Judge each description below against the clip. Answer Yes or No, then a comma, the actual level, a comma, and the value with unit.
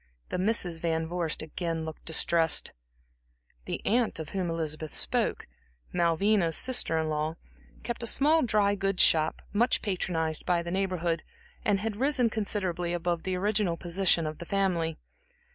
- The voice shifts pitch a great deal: No, average, 3.8 semitones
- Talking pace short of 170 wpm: Yes, average, 150 wpm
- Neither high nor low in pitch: Yes, medium, 175 Hz